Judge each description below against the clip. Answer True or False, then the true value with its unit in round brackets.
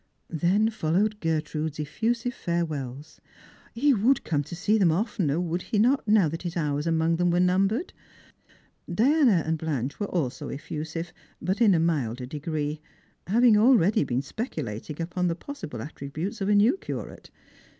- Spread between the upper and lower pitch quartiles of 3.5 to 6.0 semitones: True (5.5 semitones)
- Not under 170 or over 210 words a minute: False (160 wpm)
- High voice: False (170 Hz)